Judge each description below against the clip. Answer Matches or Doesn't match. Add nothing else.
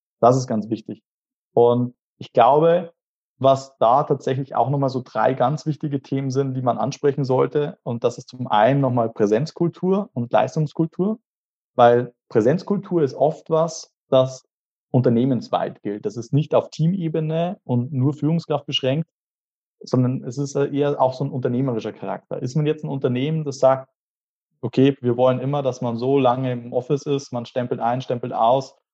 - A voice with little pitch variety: Doesn't match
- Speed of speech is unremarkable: Matches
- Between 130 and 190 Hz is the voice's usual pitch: Matches